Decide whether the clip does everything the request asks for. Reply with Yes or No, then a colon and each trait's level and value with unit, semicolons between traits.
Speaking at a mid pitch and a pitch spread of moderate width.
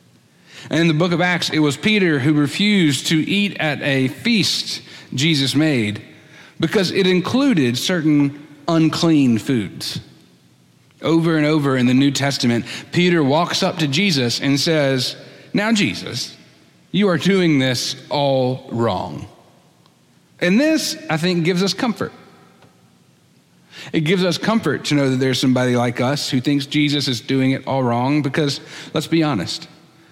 Yes: medium, 150 Hz; average, 4.4 semitones